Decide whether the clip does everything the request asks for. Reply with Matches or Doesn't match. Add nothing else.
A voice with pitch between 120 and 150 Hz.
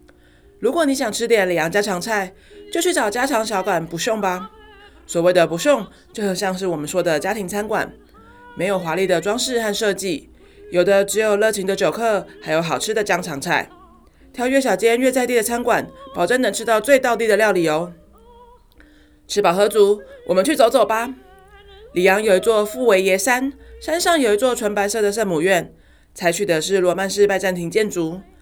Doesn't match